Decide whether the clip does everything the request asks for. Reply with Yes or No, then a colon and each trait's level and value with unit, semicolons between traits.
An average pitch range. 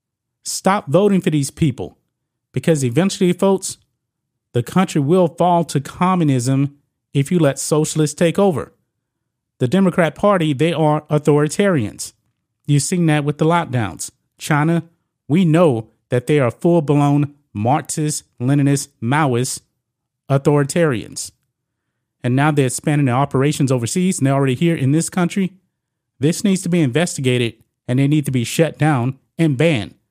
Yes: average, 4.4 semitones